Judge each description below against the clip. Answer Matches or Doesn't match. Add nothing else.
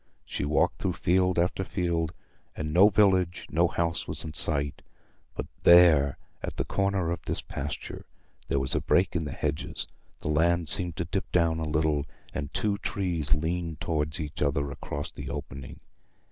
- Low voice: Matches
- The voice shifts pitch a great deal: Doesn't match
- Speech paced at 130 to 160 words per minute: Doesn't match